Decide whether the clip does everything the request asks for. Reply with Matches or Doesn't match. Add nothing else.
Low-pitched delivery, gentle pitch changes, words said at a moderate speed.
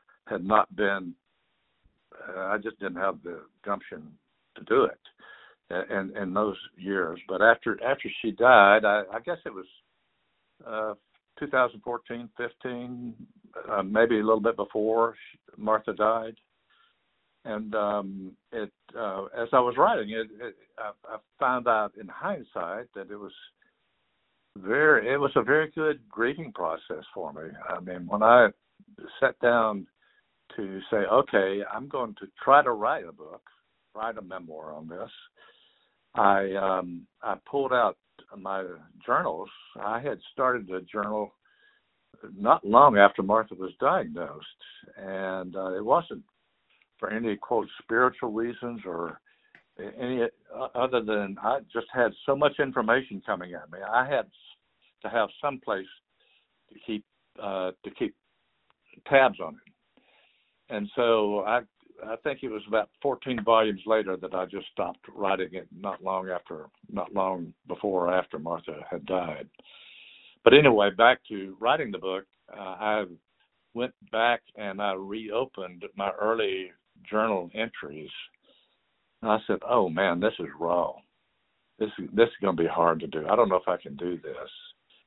Doesn't match